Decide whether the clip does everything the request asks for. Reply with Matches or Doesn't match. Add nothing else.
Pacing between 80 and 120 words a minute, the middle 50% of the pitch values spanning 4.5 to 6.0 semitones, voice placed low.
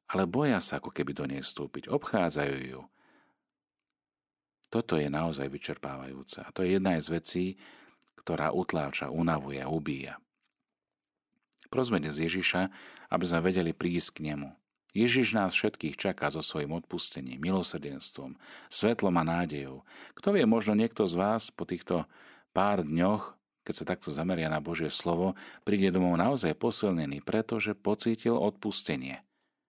Doesn't match